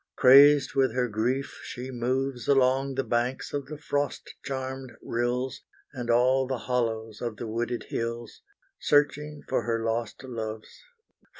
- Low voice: Yes, low, 125 Hz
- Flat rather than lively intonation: Yes, narrow, 2.3 semitones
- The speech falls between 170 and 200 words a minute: No, average, 140 wpm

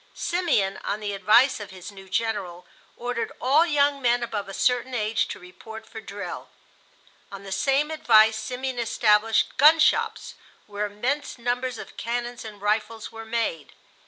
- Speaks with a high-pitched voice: Yes, high, 225 Hz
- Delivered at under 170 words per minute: Yes, average, 160 wpm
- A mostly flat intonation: No, average, 3.3 semitones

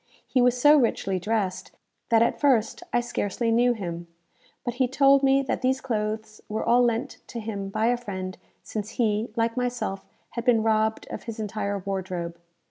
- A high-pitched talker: Yes, high, 225 Hz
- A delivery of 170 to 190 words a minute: Yes, average, 180 wpm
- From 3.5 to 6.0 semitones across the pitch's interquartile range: No, average, 3.1 semitones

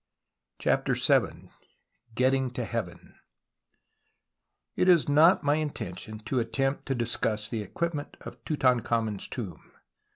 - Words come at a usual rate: No, slow, 120 wpm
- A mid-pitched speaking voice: No, low, 125 Hz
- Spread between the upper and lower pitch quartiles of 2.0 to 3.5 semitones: No, average, 4.5 semitones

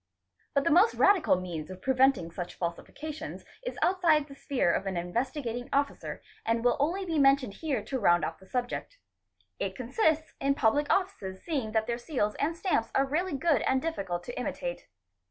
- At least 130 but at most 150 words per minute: No, average, 180 wpm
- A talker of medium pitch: No, very high, 270 Hz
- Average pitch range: No, wide, 6.9 semitones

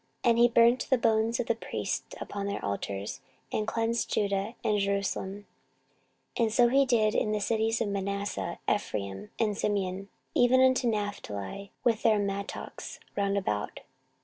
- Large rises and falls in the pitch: No, average, 2.7 semitones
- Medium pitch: No, high, 210 Hz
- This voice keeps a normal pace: Yes, average, 165 wpm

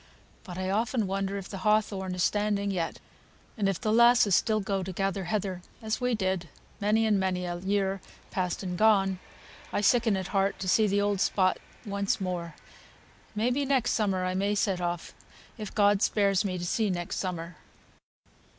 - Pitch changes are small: Yes, narrow, 2.3 semitones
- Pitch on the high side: Yes, high, 195 Hz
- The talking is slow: No, average, 185 wpm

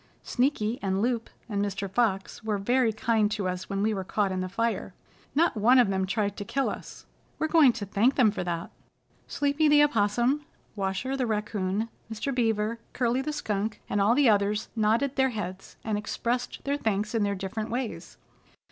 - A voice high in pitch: Yes, high, 220 Hz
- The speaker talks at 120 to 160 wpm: No, average, 190 wpm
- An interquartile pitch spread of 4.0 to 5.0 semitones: No, average, 3.6 semitones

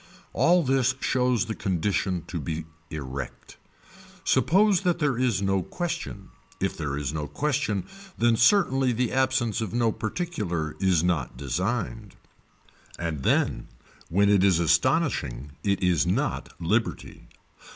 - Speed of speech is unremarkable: No, slow, 130 wpm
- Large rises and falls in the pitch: Yes, wide, 7.4 semitones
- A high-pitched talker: No, low, 105 Hz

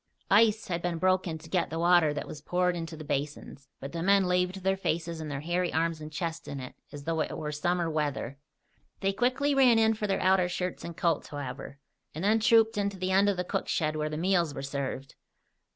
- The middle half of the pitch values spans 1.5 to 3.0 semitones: No, average, 3.8 semitones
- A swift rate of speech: Yes, fast, 230 wpm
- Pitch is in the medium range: Yes, medium, 170 Hz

